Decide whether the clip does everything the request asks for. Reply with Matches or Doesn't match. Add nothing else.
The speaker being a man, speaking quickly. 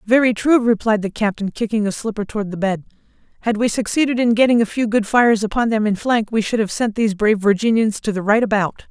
Doesn't match